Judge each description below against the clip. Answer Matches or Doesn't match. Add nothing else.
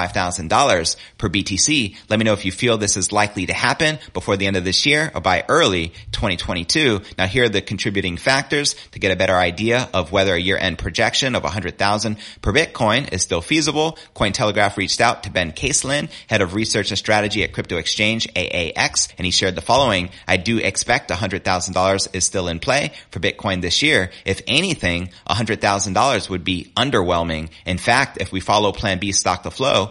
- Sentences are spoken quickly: Matches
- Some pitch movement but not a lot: Matches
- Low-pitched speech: Matches